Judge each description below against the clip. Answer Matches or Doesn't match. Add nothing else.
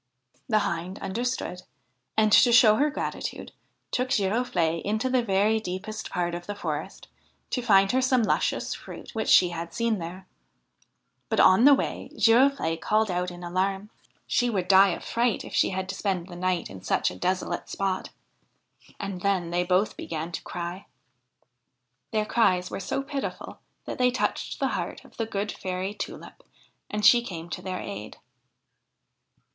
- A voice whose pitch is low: Doesn't match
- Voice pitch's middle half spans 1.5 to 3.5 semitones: Doesn't match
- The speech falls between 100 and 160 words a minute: Doesn't match